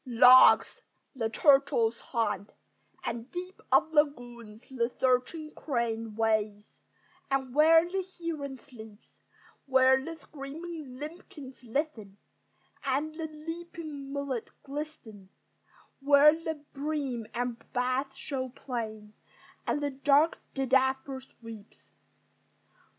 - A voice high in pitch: Yes, very high, 265 Hz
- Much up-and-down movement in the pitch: No, average, 4.2 semitones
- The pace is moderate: No, slow, 100 wpm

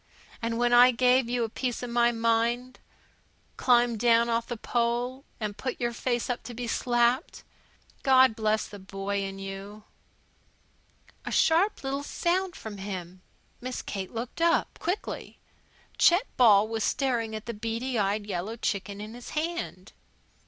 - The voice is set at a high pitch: Yes, high, 235 Hz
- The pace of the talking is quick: No, average, 155 wpm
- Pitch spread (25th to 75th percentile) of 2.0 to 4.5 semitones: Yes, average, 2.9 semitones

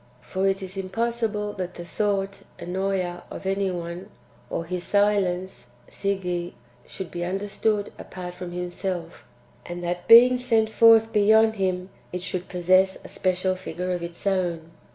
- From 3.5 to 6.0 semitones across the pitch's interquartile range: No, narrow, 2.4 semitones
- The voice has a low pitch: No, medium, 185 Hz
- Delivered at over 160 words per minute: No, average, 155 wpm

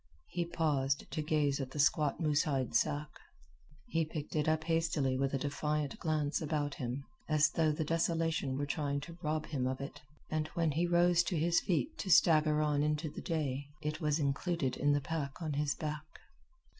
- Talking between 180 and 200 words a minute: Yes, average, 195 wpm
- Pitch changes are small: Yes, narrow, 2.1 semitones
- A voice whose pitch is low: No, medium, 150 Hz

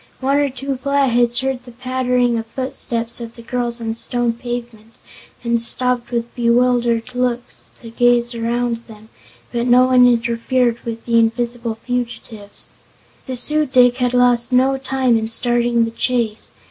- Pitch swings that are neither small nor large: No, narrow, 1.3 semitones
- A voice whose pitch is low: No, high, 240 Hz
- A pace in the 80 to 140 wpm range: No, average, 160 wpm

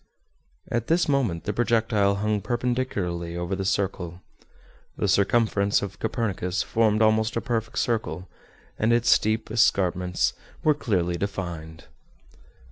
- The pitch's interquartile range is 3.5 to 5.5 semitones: Yes, average, 4.0 semitones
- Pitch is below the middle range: Yes, low, 105 Hz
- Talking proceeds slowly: Yes, slow, 125 wpm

